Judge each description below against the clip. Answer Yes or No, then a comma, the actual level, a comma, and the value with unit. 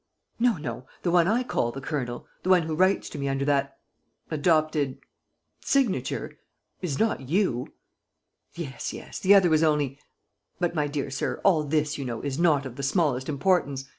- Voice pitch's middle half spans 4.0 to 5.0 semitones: Yes, average, 4.3 semitones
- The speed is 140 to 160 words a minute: No, average, 175 wpm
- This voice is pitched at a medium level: Yes, medium, 150 Hz